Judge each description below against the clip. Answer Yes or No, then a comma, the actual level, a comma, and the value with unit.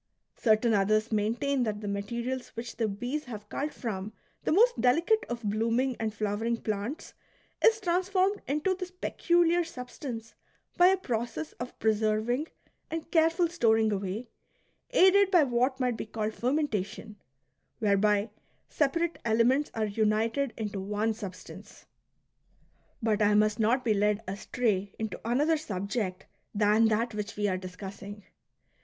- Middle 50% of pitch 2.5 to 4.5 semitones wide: No, average, 5.1 semitones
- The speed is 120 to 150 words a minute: Yes, average, 140 wpm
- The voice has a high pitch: Yes, high, 225 Hz